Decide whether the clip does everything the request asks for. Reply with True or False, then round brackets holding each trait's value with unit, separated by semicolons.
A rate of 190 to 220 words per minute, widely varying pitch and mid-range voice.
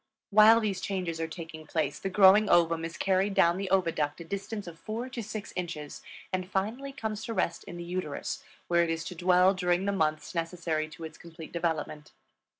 False (200 wpm; 3.2 semitones; 180 Hz)